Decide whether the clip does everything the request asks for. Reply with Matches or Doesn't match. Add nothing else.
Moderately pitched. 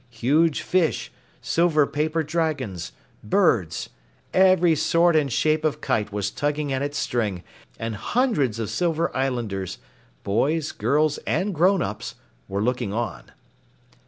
Matches